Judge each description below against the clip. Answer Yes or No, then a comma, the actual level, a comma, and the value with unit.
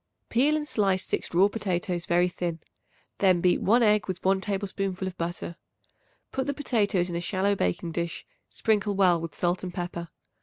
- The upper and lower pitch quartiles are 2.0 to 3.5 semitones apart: Yes, average, 2.8 semitones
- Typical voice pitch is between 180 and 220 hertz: Yes, medium, 185 Hz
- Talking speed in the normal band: Yes, average, 180 wpm